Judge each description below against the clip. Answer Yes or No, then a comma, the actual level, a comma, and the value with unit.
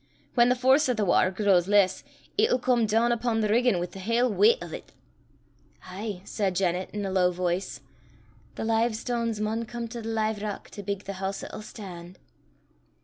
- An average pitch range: Yes, average, 3.7 semitones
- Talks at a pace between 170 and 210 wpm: Yes, average, 195 wpm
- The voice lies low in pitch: No, high, 215 Hz